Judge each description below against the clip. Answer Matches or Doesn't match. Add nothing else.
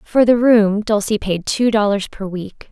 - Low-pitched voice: Doesn't match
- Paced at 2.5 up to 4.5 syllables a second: Matches